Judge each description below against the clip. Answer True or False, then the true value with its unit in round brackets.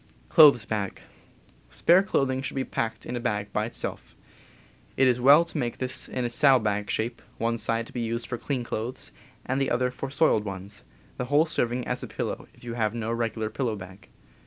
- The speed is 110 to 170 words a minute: False (205 wpm)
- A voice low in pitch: True (120 Hz)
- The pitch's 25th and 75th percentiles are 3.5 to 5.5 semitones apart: False (3.0 semitones)